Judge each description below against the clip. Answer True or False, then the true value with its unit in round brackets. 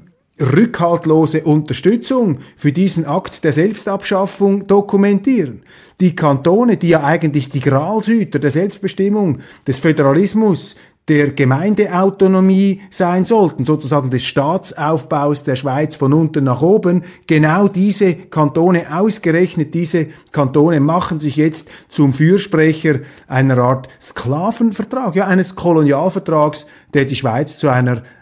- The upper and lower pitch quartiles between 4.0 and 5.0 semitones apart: True (4.6 semitones)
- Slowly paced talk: True (115 wpm)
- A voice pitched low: False (165 Hz)